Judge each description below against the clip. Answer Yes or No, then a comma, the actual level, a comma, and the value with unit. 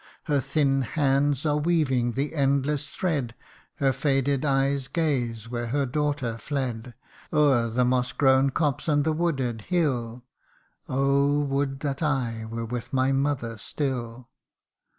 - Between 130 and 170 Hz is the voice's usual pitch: Yes, low, 135 Hz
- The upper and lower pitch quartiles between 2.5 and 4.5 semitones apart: Yes, average, 2.9 semitones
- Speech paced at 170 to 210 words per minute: No, average, 140 wpm